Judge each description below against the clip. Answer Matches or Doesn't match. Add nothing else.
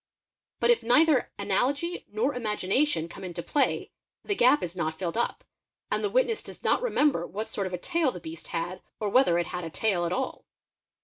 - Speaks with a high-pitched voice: Matches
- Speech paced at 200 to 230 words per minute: Matches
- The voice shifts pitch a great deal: Matches